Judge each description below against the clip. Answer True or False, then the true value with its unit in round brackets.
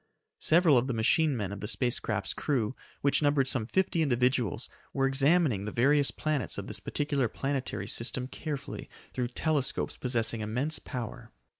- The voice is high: False (130 Hz)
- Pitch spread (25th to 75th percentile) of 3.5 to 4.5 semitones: True (3.8 semitones)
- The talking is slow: False (160 wpm)